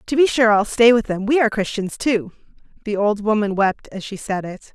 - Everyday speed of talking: No, fast, 240 wpm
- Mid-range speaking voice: No, high, 215 Hz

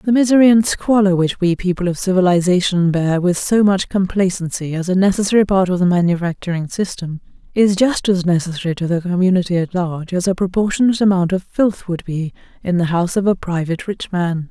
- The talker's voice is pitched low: No, medium, 185 Hz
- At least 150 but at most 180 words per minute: No, average, 195 wpm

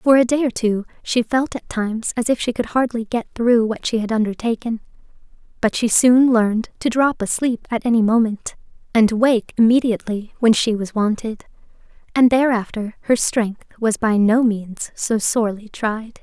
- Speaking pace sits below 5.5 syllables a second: Yes, 4.8 syllables/s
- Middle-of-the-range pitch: No, high, 225 Hz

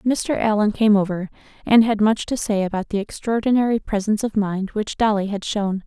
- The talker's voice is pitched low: No, high, 210 Hz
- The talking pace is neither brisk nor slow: Yes, average, 195 wpm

